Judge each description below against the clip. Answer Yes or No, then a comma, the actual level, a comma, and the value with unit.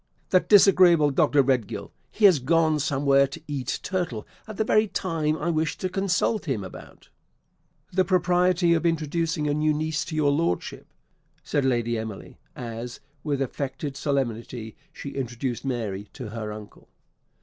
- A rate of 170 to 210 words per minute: No, average, 155 wpm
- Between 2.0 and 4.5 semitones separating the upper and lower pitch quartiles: No, average, 5.2 semitones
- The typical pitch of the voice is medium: Yes, medium, 145 Hz